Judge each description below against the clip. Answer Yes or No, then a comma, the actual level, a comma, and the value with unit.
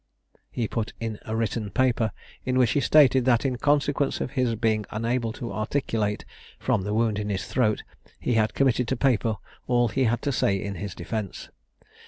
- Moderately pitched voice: No, low, 115 Hz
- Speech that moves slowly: No, average, 190 wpm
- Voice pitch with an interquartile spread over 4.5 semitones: No, average, 3.0 semitones